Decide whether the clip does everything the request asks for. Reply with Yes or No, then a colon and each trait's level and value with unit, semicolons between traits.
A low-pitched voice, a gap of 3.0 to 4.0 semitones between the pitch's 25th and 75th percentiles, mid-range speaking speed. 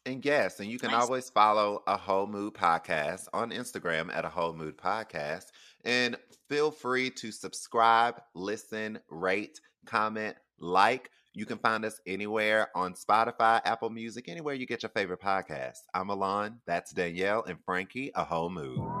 Yes: low, 110 Hz; average, 3.4 semitones; average, 160 wpm